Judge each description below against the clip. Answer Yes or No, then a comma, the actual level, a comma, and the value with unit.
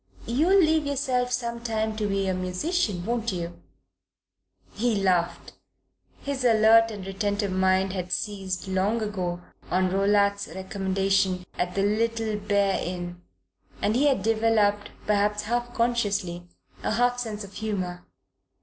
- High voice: Yes, high, 205 Hz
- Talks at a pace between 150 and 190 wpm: No, slow, 135 wpm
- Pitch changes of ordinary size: Yes, average, 3.4 semitones